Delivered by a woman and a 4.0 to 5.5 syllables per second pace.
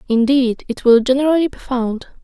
Yes: female; 5.3 syllables/s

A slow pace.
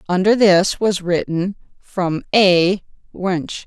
Yes: slow, 115 wpm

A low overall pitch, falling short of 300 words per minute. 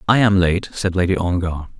Yes: very low, 90 Hz; average, 200 wpm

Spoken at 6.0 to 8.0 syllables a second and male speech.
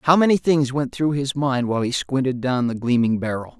No: 5.5 syllables/s; male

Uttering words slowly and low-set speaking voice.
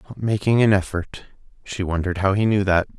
No: average, 200 wpm; low, 100 Hz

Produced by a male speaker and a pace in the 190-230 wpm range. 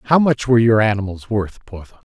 Yes: male; average, 200 wpm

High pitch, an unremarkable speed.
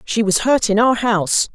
No: high, 215 Hz; fast, 235 wpm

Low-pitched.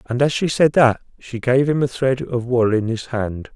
Yes: low, 125 Hz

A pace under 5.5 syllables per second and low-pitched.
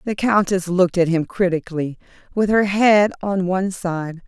No: 4.9 syllables/s; medium, 185 Hz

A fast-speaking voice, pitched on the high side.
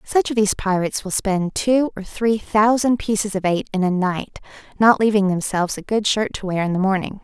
Yes: fast, 225 wpm; high, 205 Hz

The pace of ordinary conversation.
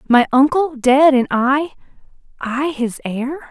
No: slow, 120 wpm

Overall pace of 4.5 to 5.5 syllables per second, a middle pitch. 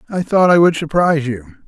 No: 5.8 syllables/s; medium, 155 Hz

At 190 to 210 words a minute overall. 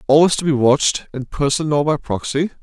Yes: fast, 205 wpm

